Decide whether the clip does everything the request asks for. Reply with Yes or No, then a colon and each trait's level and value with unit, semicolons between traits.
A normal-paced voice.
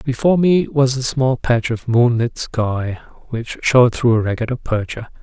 Yes: average, 170 wpm